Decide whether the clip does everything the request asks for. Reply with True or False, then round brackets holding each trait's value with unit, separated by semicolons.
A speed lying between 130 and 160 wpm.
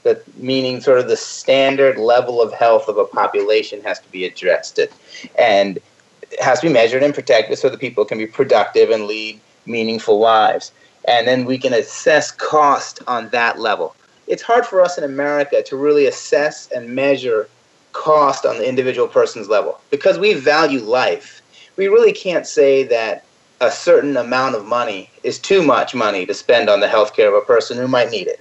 False (190 wpm)